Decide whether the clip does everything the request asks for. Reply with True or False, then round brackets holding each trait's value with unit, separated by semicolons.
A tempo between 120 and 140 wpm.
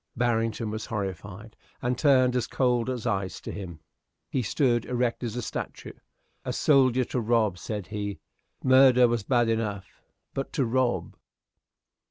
False (150 wpm)